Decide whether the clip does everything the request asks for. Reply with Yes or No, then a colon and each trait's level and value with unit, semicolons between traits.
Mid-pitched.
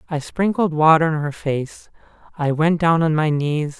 Yes: medium, 155 Hz